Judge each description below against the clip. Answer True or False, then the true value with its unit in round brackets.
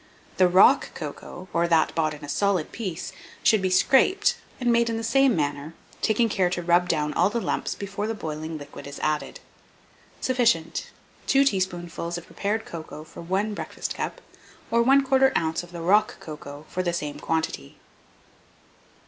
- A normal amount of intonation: False (5.7 semitones)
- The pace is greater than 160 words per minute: True (170 wpm)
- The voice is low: False (180 Hz)